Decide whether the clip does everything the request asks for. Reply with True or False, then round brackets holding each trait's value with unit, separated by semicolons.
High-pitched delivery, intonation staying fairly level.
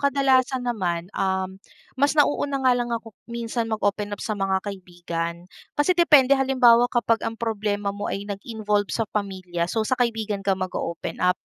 False (215 Hz; 4.2 semitones)